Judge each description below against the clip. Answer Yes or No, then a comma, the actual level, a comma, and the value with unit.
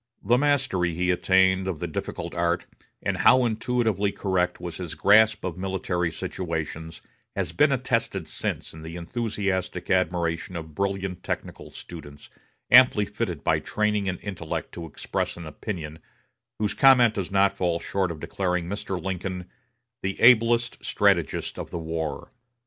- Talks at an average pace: Yes, average, 150 wpm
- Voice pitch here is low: Yes, very low, 95 Hz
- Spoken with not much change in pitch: No, average, 3.7 semitones